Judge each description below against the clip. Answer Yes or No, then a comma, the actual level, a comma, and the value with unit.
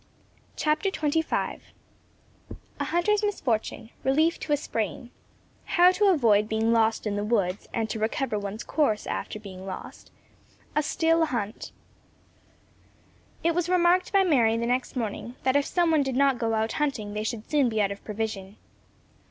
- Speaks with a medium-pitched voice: No, high, 240 Hz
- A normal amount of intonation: No, wide, 6.6 semitones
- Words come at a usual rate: Yes, average, 160 wpm